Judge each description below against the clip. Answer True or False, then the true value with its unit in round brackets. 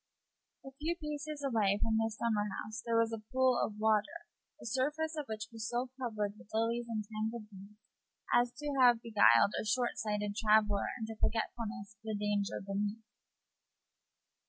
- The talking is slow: False (160 wpm)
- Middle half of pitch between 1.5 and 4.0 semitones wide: True (2.6 semitones)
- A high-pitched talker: True (225 Hz)